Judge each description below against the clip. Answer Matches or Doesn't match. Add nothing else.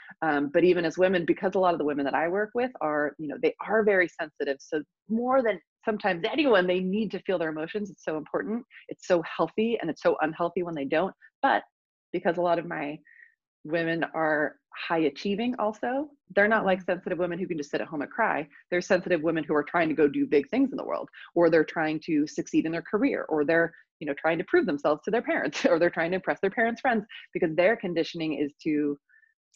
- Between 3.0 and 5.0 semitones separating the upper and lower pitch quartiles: Doesn't match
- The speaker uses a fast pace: Matches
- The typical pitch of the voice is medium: Matches